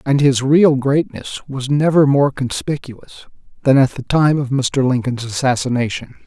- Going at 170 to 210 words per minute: No, average, 155 wpm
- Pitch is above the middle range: No, low, 135 Hz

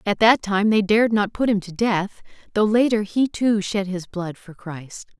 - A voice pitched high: Yes, high, 205 Hz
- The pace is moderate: No, fast, 220 wpm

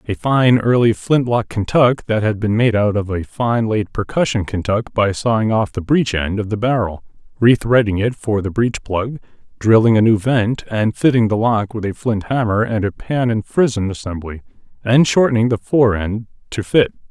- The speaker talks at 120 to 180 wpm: No, average, 195 wpm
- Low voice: Yes, low, 110 Hz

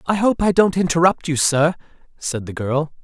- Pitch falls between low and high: Yes, medium, 160 Hz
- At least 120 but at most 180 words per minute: No, average, 200 wpm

